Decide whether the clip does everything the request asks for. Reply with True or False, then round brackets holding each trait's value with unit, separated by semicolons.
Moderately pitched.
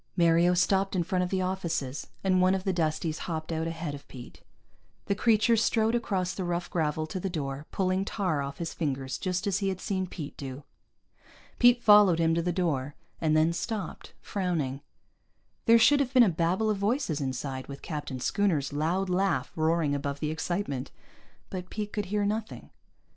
True (175 Hz)